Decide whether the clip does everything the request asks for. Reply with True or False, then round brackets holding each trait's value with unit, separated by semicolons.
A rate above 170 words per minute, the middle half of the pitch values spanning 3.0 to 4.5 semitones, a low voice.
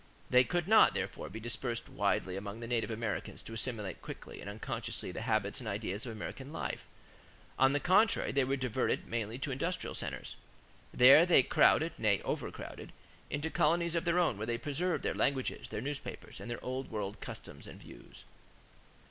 False (180 wpm; 4.9 semitones; 125 Hz)